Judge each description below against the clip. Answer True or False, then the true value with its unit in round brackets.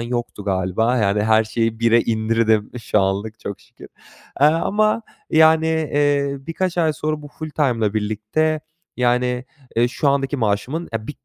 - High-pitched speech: False (125 Hz)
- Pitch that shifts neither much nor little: False (5.7 semitones)